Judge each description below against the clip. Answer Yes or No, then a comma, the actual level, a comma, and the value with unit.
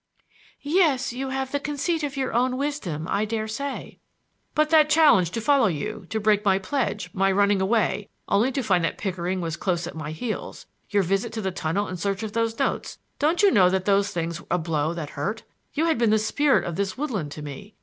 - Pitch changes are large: Yes, wide, 6.5 semitones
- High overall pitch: Yes, high, 210 Hz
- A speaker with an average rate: No, fast, 220 wpm